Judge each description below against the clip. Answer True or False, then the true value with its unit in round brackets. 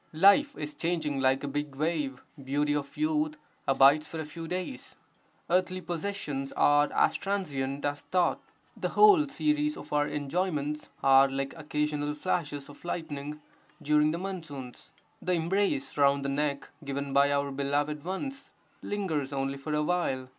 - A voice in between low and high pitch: True (150 Hz)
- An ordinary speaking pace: True (155 wpm)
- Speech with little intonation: False (4.1 semitones)